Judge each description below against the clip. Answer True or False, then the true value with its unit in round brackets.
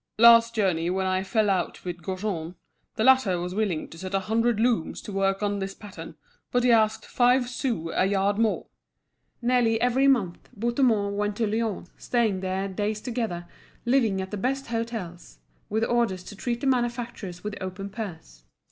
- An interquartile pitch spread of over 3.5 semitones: True (3.9 semitones)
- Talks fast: False (175 wpm)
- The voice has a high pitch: True (210 Hz)